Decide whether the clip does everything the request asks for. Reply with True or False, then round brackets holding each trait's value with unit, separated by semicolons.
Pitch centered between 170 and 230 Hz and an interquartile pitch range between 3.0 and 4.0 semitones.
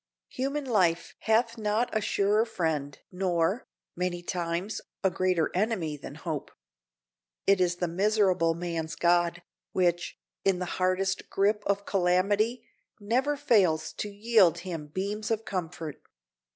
True (185 Hz; 3.6 semitones)